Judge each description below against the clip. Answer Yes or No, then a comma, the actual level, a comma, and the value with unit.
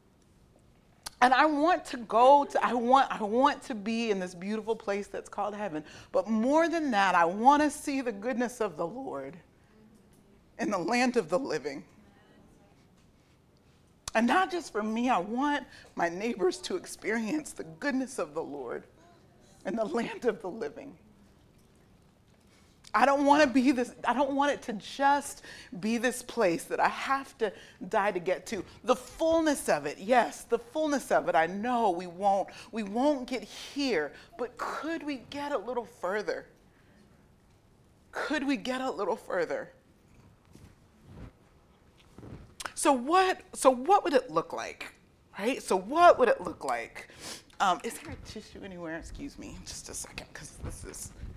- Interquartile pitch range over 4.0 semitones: Yes, average, 4.8 semitones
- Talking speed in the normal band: Yes, average, 165 wpm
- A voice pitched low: No, very high, 255 Hz